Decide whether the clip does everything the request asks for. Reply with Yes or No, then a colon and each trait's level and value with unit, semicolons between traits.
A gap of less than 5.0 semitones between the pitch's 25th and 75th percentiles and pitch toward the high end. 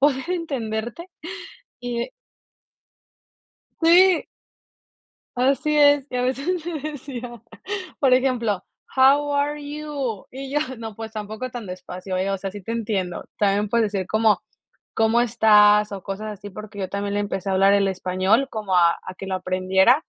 No: wide, 5.4 semitones; high, 220 Hz